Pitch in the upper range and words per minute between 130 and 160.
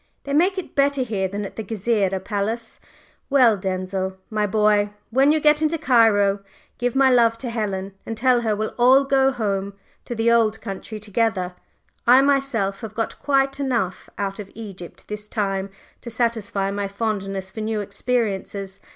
No: high, 220 Hz; average, 170 wpm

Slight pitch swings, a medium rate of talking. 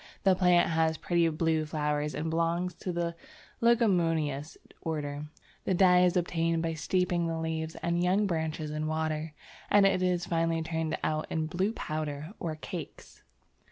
Yes: narrow, 2.2 semitones; average, 160 wpm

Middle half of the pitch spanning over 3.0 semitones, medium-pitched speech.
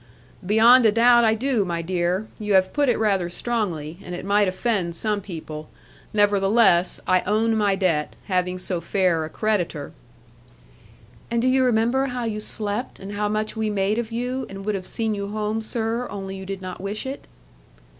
No: average, 3.4 semitones; high, 205 Hz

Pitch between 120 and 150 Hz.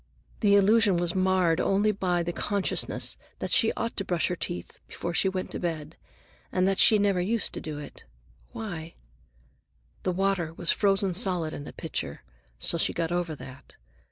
No: medium, 185 Hz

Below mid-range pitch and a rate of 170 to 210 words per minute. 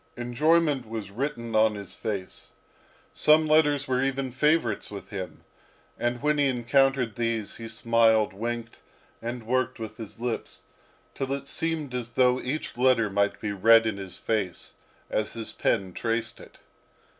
No: low, 120 Hz; average, 155 wpm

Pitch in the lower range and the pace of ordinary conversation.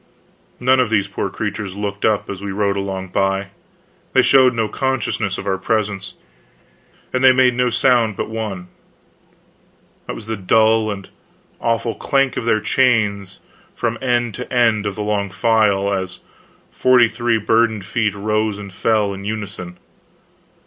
Yes: low, 110 Hz; average, 155 wpm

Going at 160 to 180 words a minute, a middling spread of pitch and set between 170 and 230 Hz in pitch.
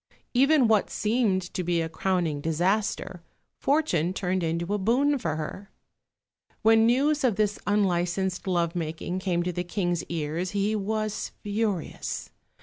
No: average, 145 wpm; average, 3.9 semitones; high, 190 Hz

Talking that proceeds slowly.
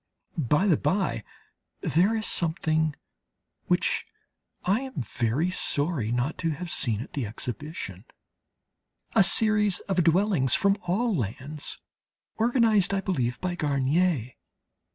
Yes: slow, 120 wpm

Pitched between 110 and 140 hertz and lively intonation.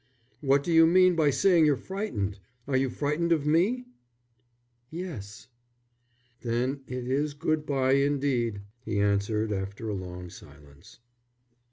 Yes: low, 135 Hz; wide, 6.8 semitones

